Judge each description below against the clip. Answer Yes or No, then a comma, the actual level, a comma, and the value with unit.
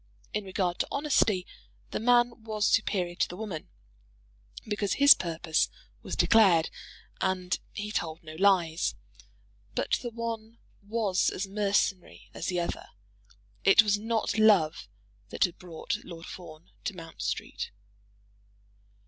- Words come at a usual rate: No, slow, 130 wpm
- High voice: Yes, high, 195 Hz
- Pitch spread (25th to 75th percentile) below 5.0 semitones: Yes, average, 4.0 semitones